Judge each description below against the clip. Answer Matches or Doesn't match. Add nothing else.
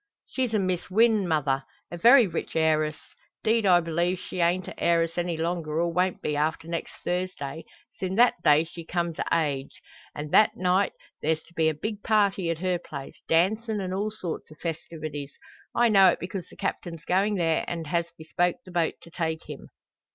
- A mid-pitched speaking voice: Matches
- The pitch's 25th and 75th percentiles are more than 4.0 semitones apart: Doesn't match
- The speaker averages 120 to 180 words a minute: Doesn't match